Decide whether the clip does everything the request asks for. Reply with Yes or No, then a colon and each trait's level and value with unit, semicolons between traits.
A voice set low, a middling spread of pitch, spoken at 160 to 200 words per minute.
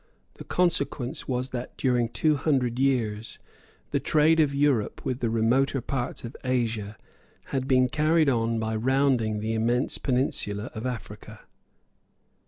No: low, 125 Hz; average, 3.2 semitones; average, 140 wpm